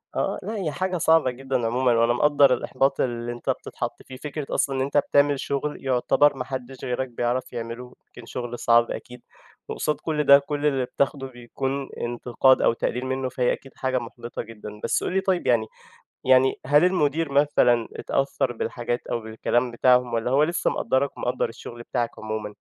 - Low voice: Yes, low, 130 Hz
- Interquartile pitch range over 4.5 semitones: No, average, 2.8 semitones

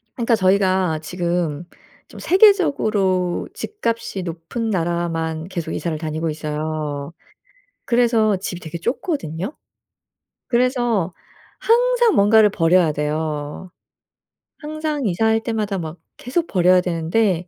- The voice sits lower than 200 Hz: Yes, medium, 185 Hz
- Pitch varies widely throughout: Yes, wide, 5.9 semitones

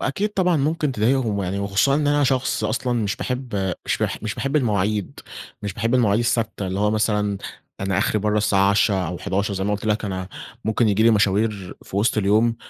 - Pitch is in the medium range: No, low, 105 Hz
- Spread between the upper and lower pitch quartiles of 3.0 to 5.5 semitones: Yes, average, 3.5 semitones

